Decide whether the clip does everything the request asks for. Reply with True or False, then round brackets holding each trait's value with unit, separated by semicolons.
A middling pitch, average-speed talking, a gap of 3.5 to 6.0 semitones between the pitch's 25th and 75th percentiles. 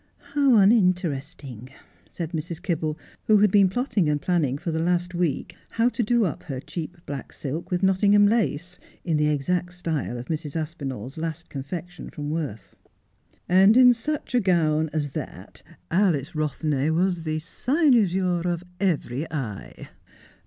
True (170 Hz; 160 wpm; 4.2 semitones)